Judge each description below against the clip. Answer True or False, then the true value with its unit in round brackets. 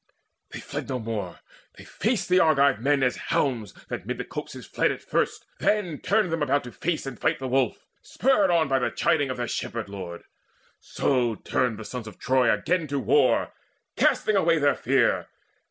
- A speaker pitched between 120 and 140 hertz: True (135 Hz)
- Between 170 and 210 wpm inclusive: True (185 wpm)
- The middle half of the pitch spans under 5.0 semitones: False (5.5 semitones)